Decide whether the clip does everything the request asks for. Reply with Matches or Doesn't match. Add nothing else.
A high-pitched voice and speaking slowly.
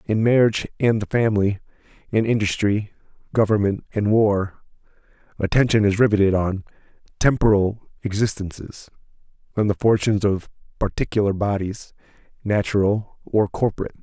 Doesn't match